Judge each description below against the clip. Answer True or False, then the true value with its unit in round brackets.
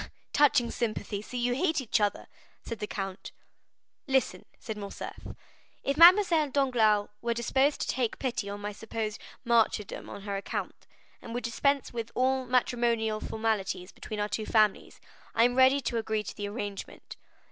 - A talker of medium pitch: False (230 Hz)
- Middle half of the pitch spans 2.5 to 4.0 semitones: True (3.5 semitones)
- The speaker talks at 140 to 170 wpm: True (160 wpm)